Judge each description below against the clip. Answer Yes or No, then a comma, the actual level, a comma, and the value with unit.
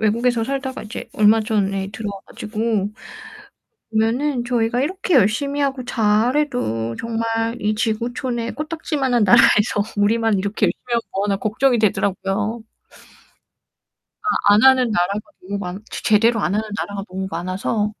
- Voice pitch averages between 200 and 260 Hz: Yes, high, 220 Hz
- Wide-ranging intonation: No, average, 3.1 semitones